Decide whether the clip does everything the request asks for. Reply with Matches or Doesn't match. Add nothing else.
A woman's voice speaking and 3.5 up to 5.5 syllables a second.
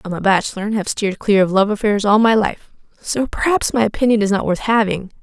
Doesn't match